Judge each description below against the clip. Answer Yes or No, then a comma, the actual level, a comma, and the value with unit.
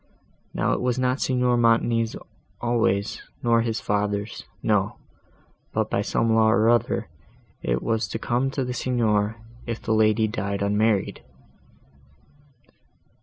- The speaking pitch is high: No, low, 115 Hz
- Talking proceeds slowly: Yes, slow, 130 wpm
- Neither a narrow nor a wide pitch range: No, narrow, 2.3 semitones